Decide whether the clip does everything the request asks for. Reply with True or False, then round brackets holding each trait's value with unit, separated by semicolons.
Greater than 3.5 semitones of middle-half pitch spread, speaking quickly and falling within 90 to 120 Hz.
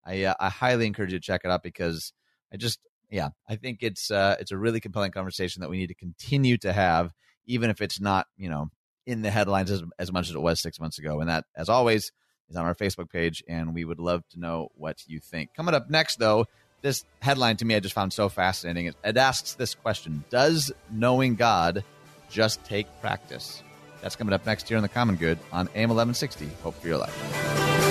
True (4.9 semitones; 225 wpm; 95 Hz)